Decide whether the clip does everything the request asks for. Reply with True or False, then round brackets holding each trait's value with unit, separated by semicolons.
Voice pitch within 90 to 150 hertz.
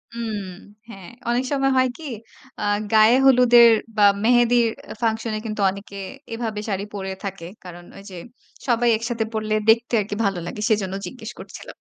False (220 Hz)